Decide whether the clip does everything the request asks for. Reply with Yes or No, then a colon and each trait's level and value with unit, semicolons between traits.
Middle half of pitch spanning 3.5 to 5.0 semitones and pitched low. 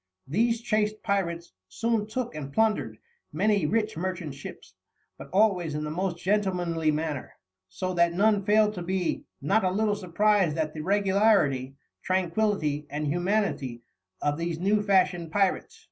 No: average, 4.6 semitones; medium, 185 Hz